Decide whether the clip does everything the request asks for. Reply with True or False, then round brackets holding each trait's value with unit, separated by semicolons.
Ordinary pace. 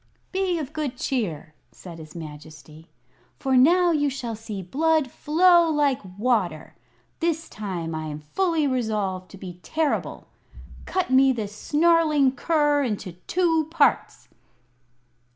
False (130 wpm)